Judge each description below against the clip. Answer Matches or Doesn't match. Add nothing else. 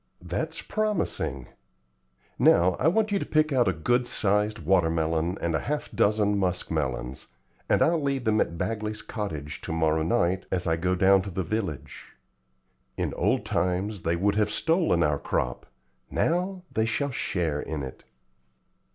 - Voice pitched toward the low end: Matches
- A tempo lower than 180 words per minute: Matches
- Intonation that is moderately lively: Doesn't match